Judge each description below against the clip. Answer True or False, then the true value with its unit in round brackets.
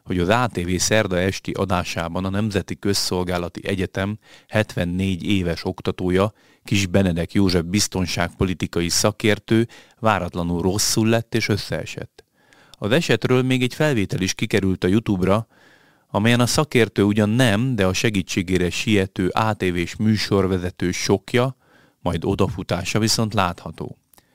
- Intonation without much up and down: False (3.5 semitones)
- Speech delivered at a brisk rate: False (120 wpm)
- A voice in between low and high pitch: False (100 Hz)